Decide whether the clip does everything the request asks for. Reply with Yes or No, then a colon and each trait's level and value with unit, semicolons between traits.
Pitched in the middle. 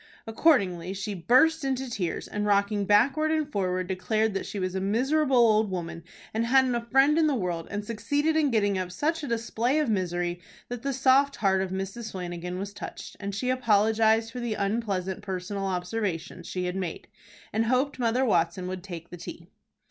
No: high, 210 Hz